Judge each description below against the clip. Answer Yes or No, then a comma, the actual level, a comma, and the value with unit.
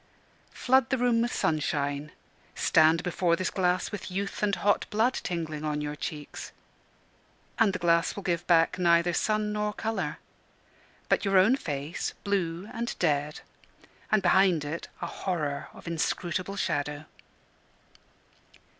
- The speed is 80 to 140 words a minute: Yes, slow, 135 wpm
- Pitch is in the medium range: Yes, medium, 175 Hz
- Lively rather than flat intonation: No, average, 4.4 semitones